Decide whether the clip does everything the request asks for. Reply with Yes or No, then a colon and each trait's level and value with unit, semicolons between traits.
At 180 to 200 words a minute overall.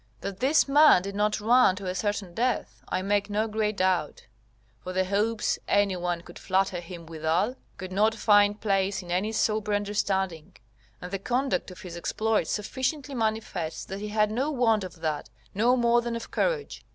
Yes: average, 185 wpm